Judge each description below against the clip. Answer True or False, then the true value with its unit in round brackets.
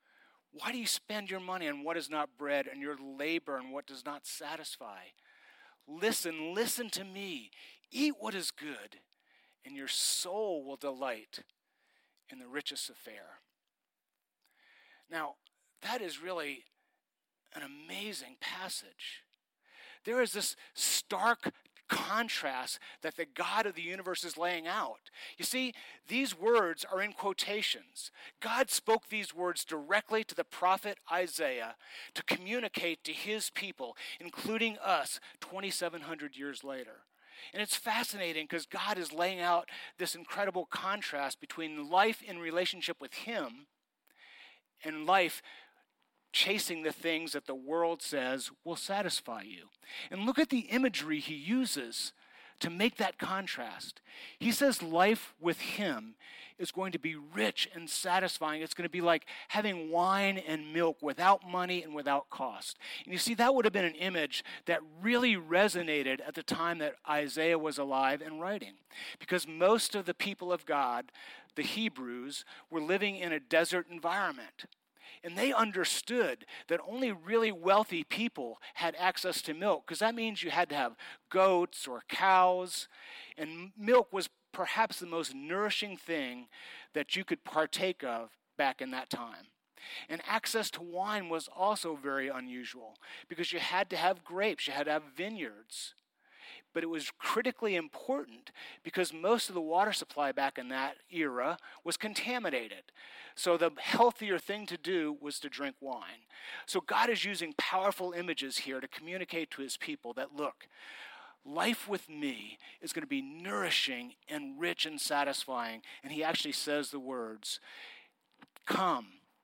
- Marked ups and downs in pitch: True (5.8 semitones)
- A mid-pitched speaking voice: True (180 Hz)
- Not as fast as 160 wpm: True (150 wpm)